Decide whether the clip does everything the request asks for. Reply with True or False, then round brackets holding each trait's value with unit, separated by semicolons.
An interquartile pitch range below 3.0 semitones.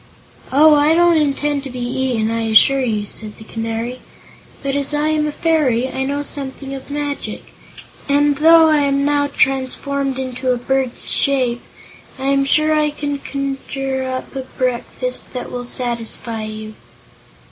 True (2.6 semitones)